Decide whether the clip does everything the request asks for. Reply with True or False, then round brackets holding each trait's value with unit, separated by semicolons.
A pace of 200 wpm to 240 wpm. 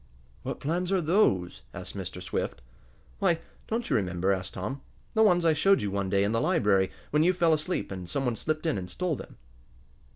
True (205 wpm)